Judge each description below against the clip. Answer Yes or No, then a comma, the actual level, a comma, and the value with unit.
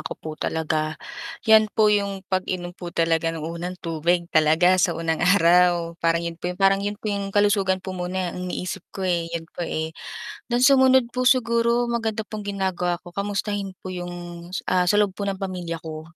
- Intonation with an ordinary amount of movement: Yes, average, 3.1 semitones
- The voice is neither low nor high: Yes, medium, 180 Hz